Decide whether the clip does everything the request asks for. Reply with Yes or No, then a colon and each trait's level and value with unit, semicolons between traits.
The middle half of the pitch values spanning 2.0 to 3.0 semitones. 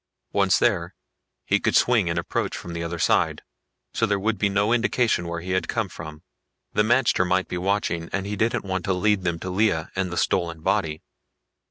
No: average, 3.5 semitones